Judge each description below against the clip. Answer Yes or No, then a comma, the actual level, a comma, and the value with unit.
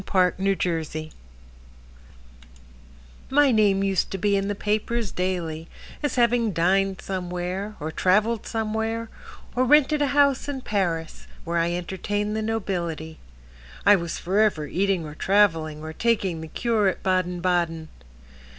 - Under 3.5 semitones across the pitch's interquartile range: No, average, 4.2 semitones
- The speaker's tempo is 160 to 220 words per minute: No, slow, 135 wpm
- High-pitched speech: Yes, high, 195 Hz